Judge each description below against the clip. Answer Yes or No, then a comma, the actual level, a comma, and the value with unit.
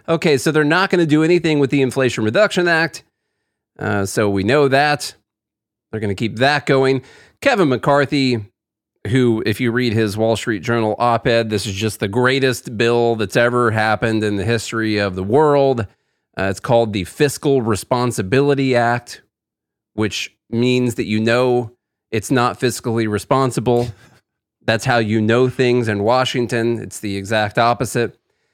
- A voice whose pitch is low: Yes, low, 120 Hz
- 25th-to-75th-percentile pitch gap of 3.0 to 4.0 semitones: Yes, average, 3.3 semitones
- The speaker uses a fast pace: No, average, 165 wpm